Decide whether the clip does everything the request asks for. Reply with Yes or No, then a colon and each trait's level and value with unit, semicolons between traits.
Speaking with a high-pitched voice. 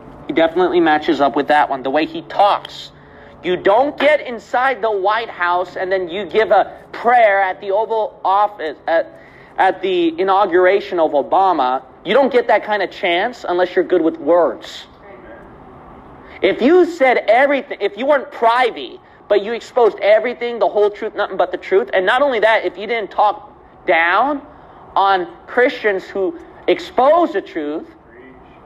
Yes: high, 220 Hz